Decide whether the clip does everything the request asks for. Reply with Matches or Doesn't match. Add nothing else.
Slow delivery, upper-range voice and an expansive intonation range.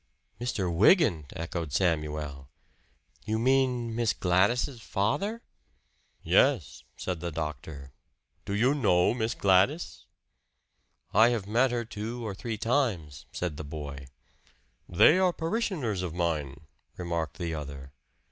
Doesn't match